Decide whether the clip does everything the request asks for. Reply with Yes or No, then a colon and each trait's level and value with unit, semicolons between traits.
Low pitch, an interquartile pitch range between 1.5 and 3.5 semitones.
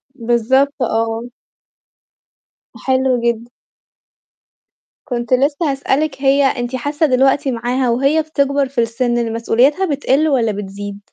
No: very high, 260 Hz; average, 3.0 semitones